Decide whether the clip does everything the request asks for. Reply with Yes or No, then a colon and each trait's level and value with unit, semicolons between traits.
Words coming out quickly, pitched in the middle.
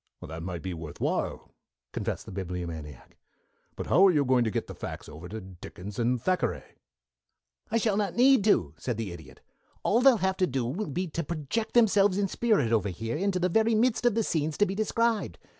Yes: fast, 210 wpm; medium, 155 Hz